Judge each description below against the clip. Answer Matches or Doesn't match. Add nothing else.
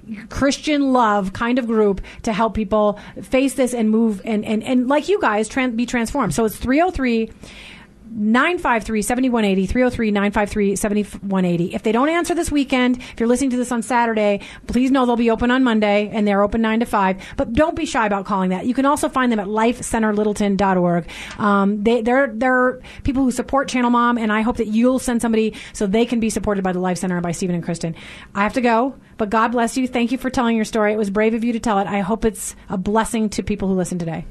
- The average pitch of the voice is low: Doesn't match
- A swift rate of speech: Matches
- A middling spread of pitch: Matches